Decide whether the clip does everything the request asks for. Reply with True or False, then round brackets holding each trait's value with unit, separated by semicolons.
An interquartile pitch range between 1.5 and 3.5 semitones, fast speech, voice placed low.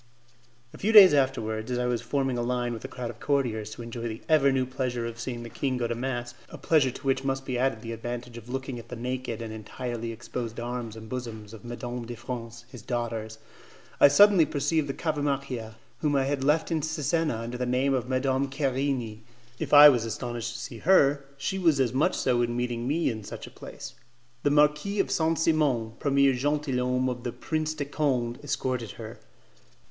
True (3.0 semitones; 210 wpm; 125 Hz)